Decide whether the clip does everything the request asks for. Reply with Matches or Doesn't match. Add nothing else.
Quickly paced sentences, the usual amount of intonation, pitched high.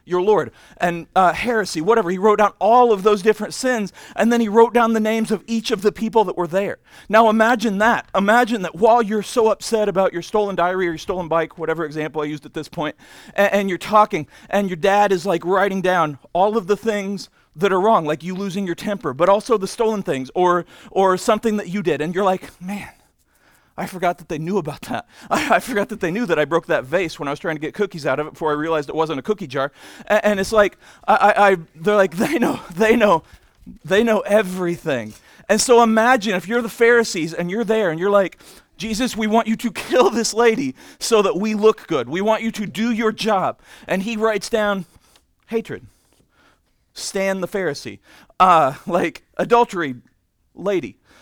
Matches